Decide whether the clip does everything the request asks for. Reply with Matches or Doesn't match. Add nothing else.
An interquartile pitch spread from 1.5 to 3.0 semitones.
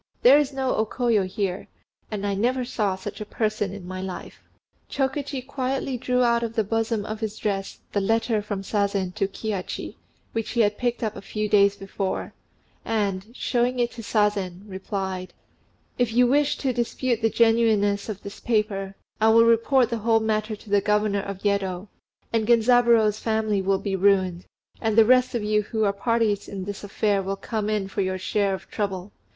Matches